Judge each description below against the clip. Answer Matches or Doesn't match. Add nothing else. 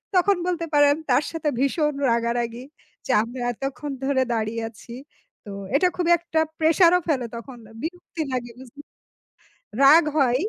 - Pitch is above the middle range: Matches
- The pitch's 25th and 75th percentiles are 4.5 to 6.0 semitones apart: Matches